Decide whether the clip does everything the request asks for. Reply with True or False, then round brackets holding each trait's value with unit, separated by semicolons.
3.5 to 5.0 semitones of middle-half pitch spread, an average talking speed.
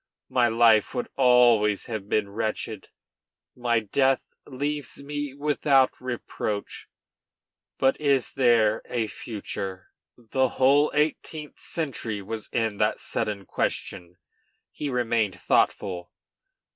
False (4.1 semitones; 105 wpm)